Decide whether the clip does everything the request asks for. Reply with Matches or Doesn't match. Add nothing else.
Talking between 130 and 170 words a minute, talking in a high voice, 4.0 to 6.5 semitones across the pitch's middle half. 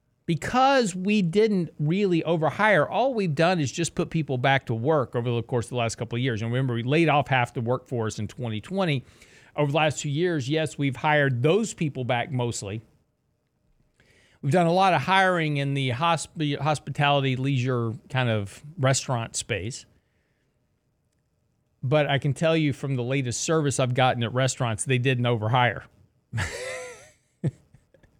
Doesn't match